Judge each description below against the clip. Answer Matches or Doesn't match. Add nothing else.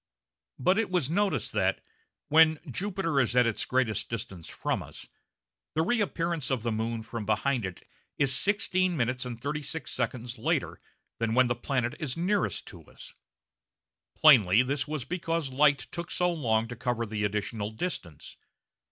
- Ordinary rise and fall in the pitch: Doesn't match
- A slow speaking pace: Doesn't match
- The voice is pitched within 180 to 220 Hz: Doesn't match